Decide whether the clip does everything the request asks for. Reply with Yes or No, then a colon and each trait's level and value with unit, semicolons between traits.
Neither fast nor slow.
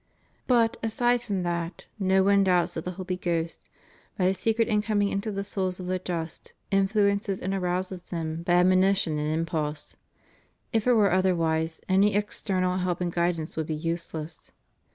Yes: average, 165 wpm